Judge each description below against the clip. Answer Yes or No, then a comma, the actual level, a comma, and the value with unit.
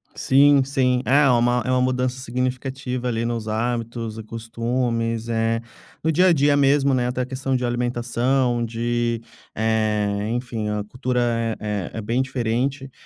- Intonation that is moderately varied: No, narrow, 2.1 semitones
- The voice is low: Yes, low, 120 Hz